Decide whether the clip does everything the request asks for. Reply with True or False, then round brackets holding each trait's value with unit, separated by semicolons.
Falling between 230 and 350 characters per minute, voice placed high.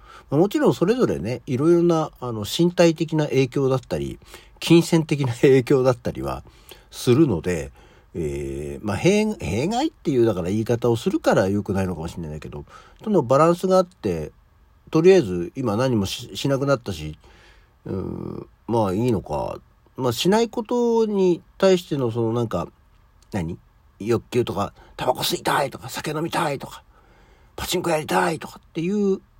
False (330 characters per minute; 125 Hz)